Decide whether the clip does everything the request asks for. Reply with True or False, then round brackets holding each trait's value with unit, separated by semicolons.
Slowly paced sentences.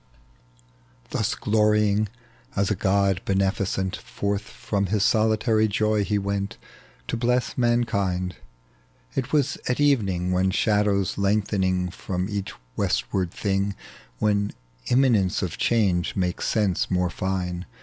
True (120 wpm)